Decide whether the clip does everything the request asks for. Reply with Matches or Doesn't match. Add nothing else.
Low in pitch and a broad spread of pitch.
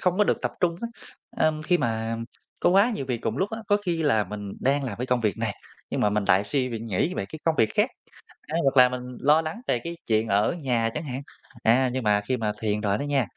Matches